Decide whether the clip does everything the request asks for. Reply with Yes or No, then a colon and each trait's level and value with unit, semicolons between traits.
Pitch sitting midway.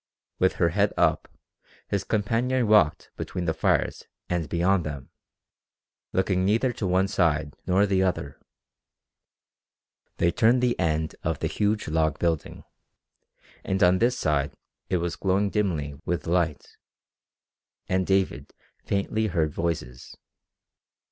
No: very low, 90 Hz